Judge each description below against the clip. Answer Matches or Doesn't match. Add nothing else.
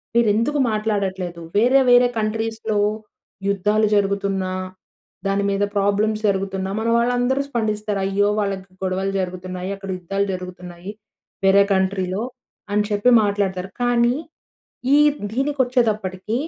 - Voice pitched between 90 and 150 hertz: Doesn't match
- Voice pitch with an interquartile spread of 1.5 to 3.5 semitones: Matches